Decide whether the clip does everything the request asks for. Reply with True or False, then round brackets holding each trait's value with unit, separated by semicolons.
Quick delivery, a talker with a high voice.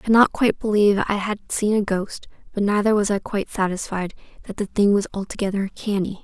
True (210 wpm; 205 Hz)